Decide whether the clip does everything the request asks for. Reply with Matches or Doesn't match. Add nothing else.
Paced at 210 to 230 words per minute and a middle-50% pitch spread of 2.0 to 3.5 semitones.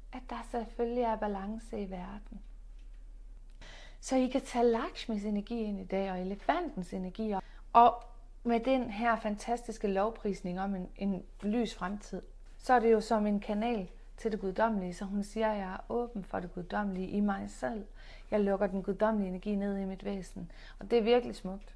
Doesn't match